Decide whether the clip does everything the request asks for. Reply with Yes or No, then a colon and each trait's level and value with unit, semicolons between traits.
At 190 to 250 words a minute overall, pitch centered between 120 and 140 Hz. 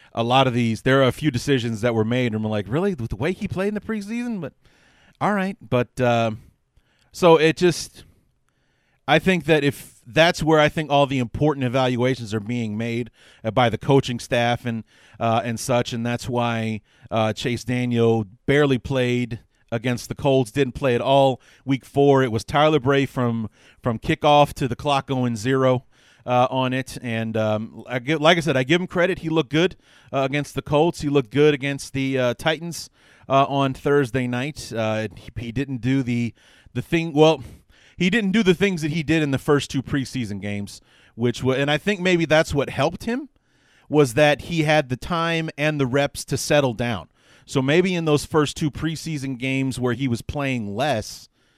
Yes: average, 200 wpm; low, 135 Hz